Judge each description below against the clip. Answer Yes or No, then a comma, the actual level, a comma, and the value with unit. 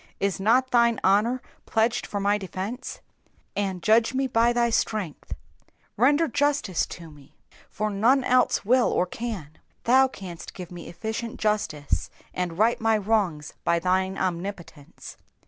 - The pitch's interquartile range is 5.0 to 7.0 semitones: No, average, 4.6 semitones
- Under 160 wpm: Yes, average, 145 wpm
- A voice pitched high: Yes, high, 210 Hz